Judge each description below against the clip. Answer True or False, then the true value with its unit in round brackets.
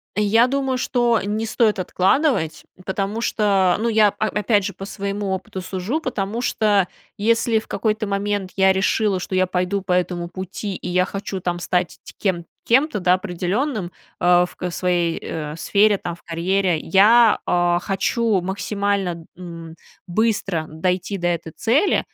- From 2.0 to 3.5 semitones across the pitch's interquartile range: True (3.2 semitones)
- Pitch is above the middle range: True (195 Hz)